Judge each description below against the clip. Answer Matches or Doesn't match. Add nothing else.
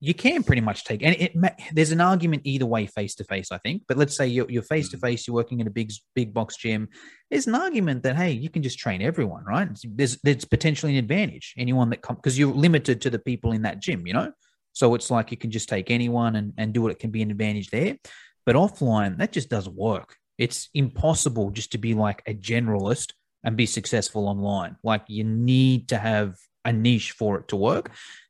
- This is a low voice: Matches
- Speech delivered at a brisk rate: Matches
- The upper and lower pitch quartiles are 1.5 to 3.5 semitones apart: Doesn't match